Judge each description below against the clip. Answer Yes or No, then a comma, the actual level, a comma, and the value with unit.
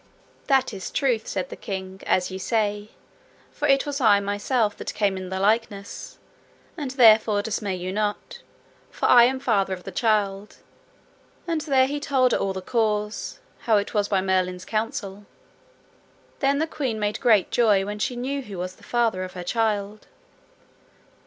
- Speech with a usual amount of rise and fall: Yes, average, 3.9 semitones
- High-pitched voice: Yes, high, 210 Hz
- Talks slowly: No, average, 170 wpm